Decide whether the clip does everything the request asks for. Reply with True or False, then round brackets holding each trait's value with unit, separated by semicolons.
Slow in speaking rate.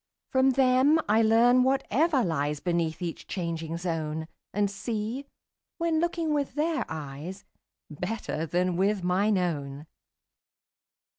True (125 wpm)